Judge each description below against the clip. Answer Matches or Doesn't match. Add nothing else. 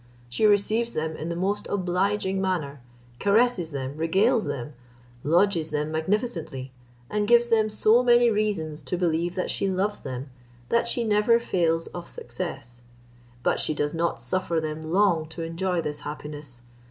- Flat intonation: Doesn't match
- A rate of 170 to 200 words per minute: Doesn't match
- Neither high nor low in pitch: Matches